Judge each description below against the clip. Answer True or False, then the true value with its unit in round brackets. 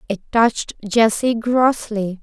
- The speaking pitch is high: True (225 Hz)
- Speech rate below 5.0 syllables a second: True (4.0 syllables/s)